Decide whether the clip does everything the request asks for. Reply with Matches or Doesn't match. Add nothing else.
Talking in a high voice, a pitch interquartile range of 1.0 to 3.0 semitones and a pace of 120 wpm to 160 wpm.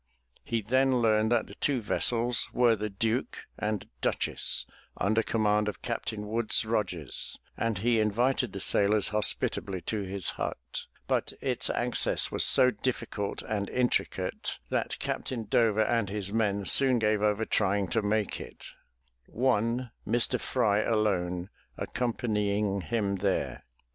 Doesn't match